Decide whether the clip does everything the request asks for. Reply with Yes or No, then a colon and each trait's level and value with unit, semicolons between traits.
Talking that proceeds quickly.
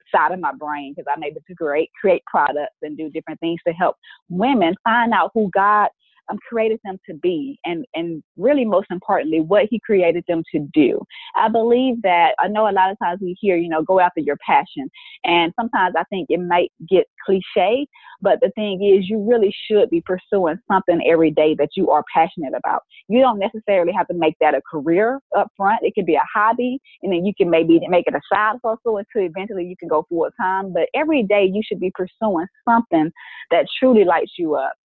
Yes: fast, 215 wpm